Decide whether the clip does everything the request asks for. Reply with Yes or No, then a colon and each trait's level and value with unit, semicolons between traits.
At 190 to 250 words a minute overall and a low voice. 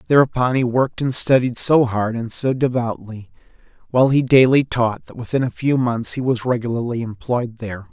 No: average, 180 wpm; low, 125 Hz